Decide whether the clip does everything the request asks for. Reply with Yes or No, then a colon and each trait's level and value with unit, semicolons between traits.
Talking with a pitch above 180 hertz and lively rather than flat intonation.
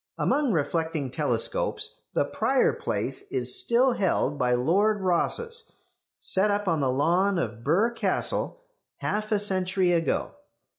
Yes: high, 190 Hz; wide, 6.6 semitones